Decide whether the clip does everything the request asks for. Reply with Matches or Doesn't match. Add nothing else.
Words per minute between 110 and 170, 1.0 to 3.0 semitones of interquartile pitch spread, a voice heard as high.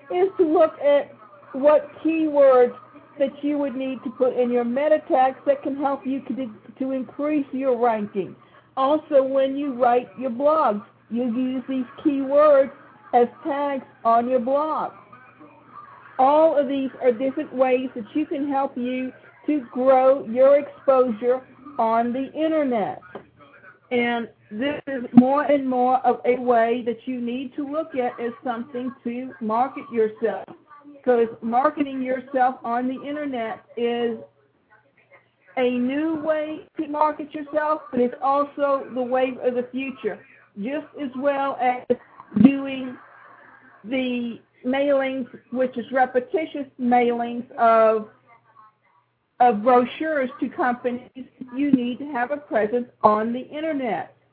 Matches